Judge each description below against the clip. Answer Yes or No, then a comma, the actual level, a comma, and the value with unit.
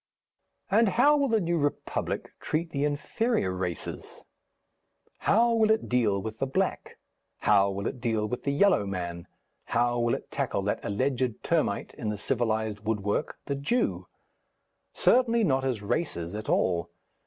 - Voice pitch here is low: Yes, low, 125 Hz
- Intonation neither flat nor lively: No, wide, 8.8 semitones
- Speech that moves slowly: No, average, 155 wpm